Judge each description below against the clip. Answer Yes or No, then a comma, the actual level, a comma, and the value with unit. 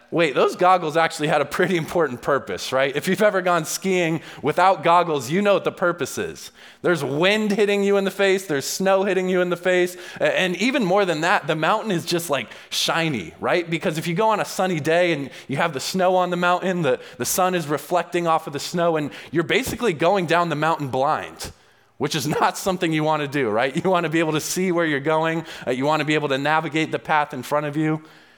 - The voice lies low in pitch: No, medium, 170 Hz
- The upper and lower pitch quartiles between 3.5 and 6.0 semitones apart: No, average, 3.1 semitones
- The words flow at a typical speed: No, fast, 240 wpm